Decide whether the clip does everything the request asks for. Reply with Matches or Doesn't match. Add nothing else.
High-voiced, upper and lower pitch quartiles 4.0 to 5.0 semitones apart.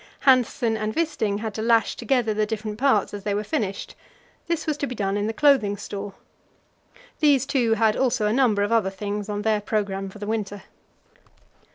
Doesn't match